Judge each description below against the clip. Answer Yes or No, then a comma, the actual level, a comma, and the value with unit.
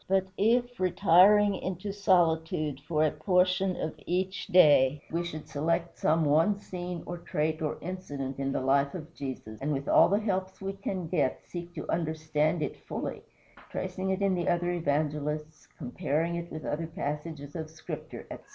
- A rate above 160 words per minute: Yes, average, 170 wpm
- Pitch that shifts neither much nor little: Yes, average, 3.5 semitones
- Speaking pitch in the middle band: Yes, medium, 165 Hz